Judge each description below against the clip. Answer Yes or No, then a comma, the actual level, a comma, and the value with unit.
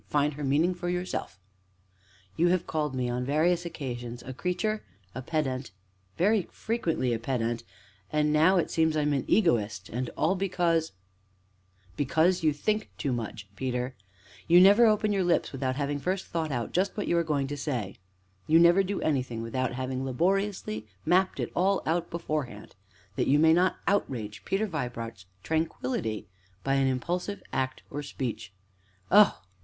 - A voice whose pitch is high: No, medium, 150 Hz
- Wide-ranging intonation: Yes, wide, 5.9 semitones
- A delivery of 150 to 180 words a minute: Yes, average, 165 wpm